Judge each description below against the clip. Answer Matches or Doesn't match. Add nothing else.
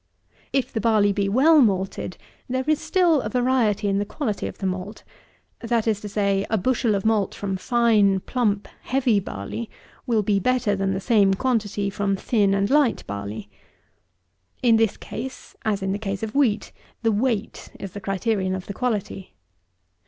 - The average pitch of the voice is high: Matches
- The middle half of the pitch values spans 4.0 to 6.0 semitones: Doesn't match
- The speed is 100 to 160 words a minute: Doesn't match